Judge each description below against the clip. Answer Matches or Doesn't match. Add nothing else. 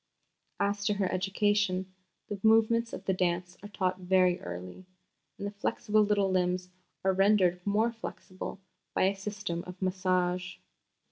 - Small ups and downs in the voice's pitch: Matches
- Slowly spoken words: Doesn't match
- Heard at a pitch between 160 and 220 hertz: Matches